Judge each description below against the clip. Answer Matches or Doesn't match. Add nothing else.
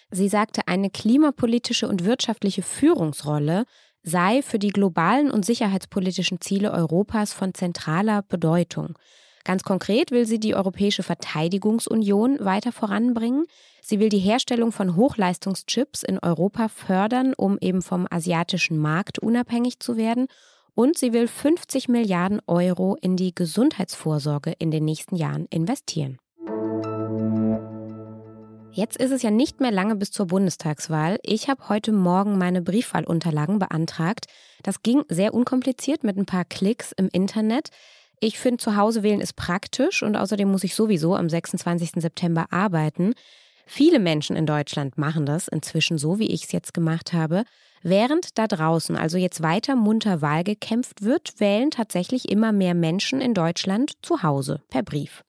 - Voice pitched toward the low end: Doesn't match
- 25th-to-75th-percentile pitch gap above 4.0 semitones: Matches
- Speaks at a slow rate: Doesn't match